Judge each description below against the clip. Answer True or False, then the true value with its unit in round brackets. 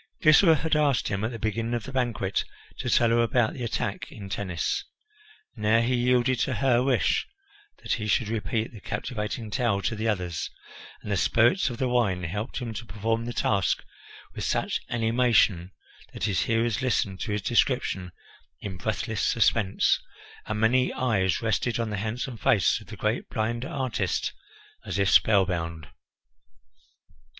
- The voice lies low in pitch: True (115 Hz)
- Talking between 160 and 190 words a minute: True (165 wpm)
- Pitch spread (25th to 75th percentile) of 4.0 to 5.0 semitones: False (3.2 semitones)